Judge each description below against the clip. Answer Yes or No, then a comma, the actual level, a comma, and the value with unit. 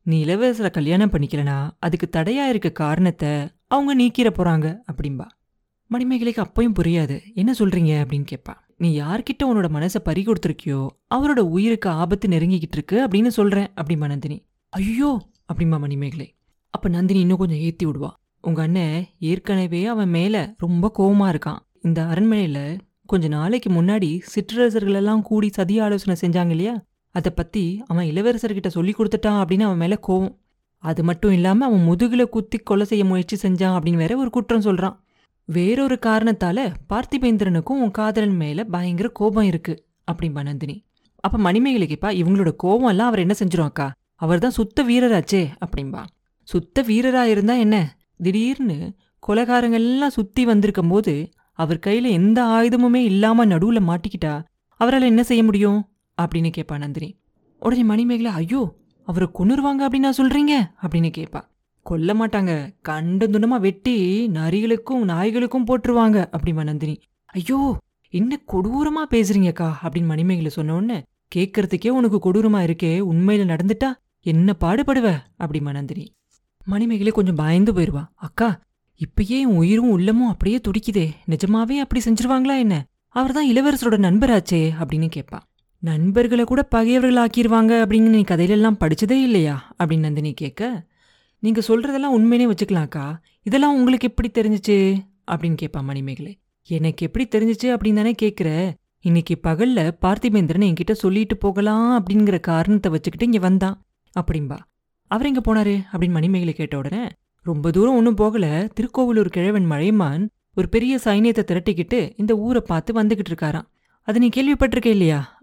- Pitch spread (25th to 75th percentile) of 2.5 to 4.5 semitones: No, average, 5.1 semitones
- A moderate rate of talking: No, fast, 135 wpm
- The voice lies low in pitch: No, high, 200 Hz